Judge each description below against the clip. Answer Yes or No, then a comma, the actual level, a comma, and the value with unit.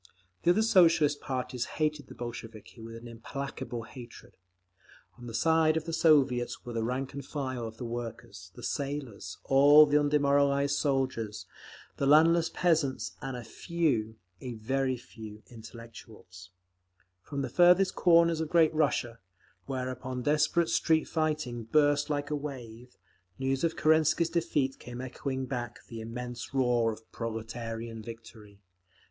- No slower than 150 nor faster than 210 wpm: No, average, 140 wpm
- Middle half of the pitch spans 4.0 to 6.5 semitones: Yes, average, 4.5 semitones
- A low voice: Yes, low, 130 Hz